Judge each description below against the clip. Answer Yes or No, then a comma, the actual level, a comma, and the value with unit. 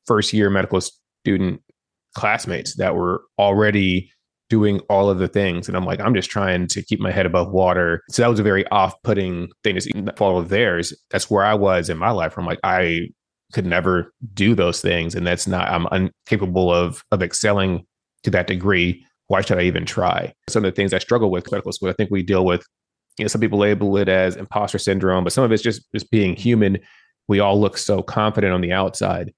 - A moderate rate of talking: No, fast, 220 wpm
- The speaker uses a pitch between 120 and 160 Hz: No, very low, 95 Hz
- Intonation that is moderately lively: No, narrow, 2.3 semitones